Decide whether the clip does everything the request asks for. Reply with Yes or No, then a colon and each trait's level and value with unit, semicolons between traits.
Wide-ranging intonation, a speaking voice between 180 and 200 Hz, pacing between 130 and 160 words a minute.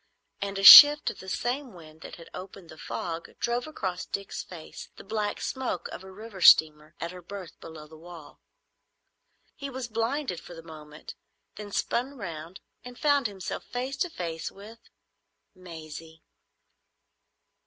Yes: wide, 6.4 semitones; high, 190 Hz; average, 155 wpm